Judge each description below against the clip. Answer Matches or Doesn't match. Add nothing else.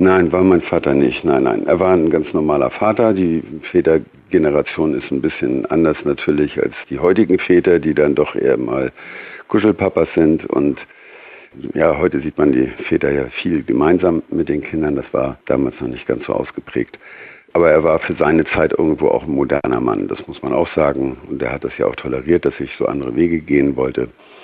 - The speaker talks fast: Matches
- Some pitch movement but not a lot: Matches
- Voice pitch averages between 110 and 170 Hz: Doesn't match